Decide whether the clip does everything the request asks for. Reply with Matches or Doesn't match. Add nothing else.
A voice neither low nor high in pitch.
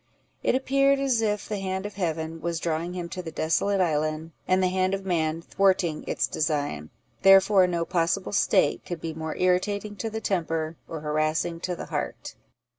Matches